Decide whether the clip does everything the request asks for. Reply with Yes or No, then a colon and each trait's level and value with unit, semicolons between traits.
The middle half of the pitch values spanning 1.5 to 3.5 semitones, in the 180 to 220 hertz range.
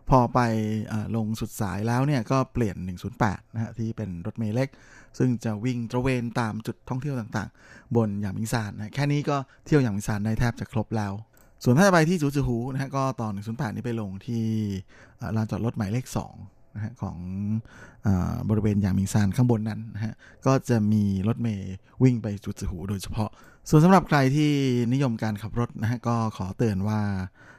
No: average, 2.8 semitones; low, 115 Hz